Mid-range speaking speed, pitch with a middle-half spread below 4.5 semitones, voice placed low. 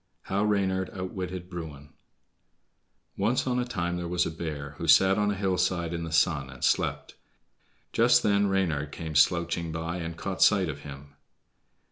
Yes: average, 165 wpm; average, 3.2 semitones; very low, 85 Hz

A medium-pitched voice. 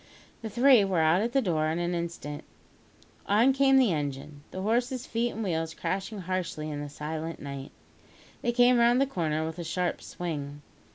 Yes: medium, 175 Hz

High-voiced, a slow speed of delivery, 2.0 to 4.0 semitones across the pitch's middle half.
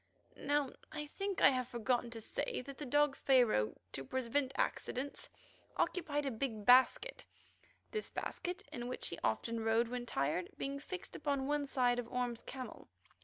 No: very high, 255 Hz; average, 165 wpm; average, 3.5 semitones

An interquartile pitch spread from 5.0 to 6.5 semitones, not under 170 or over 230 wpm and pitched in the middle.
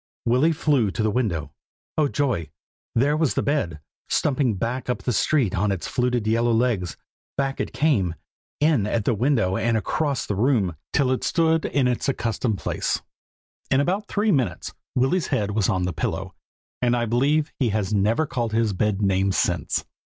No: average, 5.3 semitones; average, 180 wpm; low, 120 Hz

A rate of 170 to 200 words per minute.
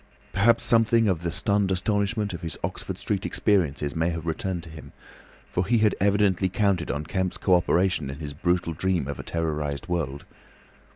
Yes: average, 180 wpm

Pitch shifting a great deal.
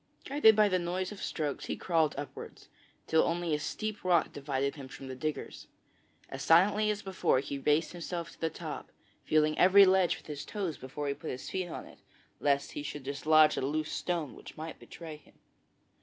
No: average, 4.1 semitones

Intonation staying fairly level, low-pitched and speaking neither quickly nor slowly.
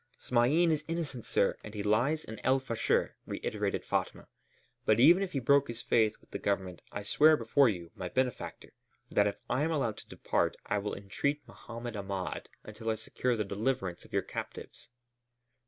No: wide, 5.4 semitones; low, 115 Hz; average, 180 wpm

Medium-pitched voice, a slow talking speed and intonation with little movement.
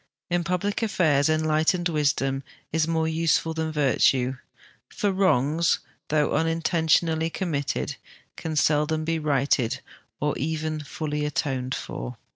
Yes: medium, 155 Hz; slow, 120 wpm; narrow, 2.2 semitones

